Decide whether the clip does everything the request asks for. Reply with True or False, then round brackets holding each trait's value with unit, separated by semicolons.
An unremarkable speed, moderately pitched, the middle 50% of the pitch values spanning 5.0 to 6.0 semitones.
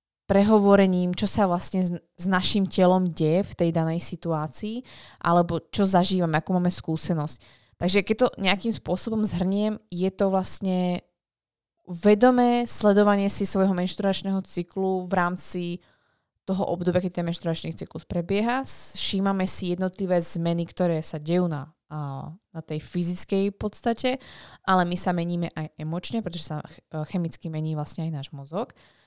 False (140 wpm; 180 Hz; 2.7 semitones)